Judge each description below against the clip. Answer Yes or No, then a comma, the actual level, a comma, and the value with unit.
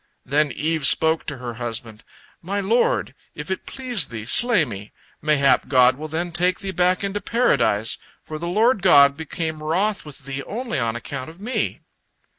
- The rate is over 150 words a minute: Yes, average, 175 wpm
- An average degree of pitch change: No, wide, 6.3 semitones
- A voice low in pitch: No, medium, 160 Hz